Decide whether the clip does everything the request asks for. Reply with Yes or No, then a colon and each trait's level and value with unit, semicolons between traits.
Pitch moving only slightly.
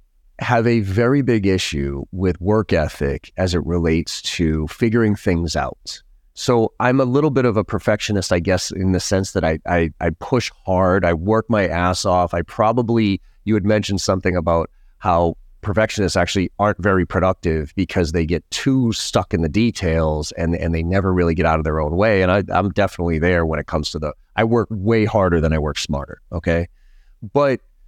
No: average, 4.2 semitones